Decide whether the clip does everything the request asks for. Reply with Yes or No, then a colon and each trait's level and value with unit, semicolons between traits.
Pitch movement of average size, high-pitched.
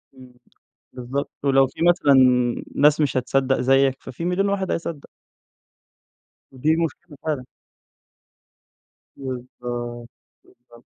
No: average, 3.3 semitones; low, 135 Hz